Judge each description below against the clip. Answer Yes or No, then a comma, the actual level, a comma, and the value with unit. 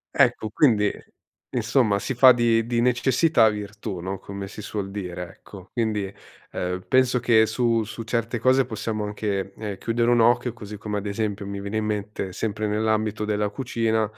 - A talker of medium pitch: No, low, 110 Hz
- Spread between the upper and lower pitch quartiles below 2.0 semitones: No, narrow, 2.4 semitones